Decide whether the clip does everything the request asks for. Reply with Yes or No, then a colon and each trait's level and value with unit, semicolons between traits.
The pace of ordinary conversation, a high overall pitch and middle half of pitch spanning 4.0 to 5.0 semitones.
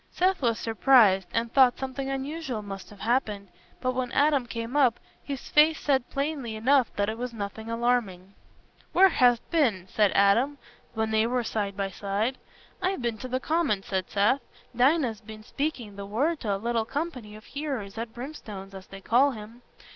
Yes: average, 180 wpm; high, 235 Hz; average, 4.4 semitones